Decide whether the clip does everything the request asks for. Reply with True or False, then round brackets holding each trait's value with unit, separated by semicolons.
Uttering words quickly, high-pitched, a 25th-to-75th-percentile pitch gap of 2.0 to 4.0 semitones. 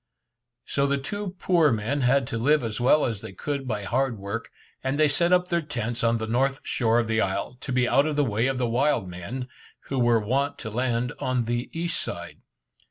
False (225 wpm; 125 Hz; 3.5 semitones)